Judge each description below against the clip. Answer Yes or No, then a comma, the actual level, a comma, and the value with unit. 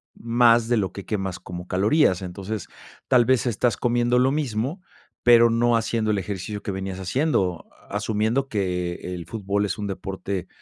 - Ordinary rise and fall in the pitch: Yes, average, 3.9 semitones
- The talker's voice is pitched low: Yes, low, 105 Hz